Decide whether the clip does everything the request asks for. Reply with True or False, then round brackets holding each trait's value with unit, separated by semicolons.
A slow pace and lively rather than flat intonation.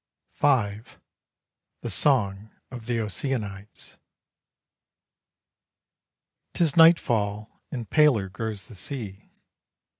False (80 wpm; 4.8 semitones)